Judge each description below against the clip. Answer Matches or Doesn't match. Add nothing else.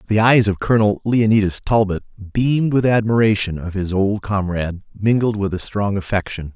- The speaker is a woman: Doesn't match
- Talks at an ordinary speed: Matches